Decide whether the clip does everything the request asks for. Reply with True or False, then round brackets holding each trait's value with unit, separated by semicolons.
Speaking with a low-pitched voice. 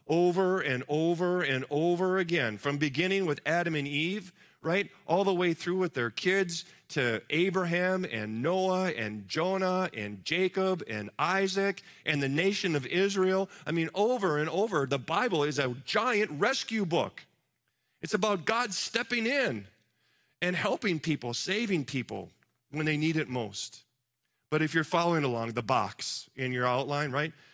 False (165 Hz)